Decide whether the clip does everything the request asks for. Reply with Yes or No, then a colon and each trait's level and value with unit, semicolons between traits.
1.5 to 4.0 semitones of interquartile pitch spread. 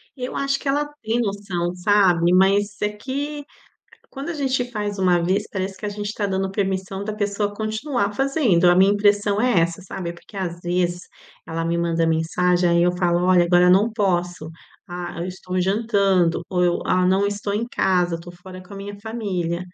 Yes: average, 2.9 semitones